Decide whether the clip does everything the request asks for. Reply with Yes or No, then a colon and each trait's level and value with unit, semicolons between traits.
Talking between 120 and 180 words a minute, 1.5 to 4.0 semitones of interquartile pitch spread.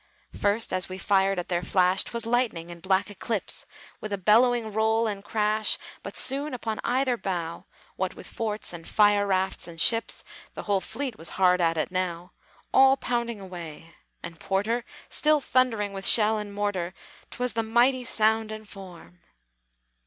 Yes: average, 170 wpm; average, 3.7 semitones